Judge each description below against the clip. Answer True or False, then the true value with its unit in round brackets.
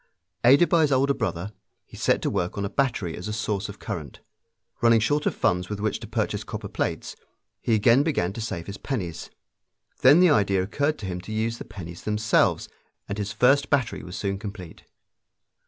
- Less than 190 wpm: False (200 wpm)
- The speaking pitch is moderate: False (105 Hz)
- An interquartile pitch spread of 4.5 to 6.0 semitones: True (5.2 semitones)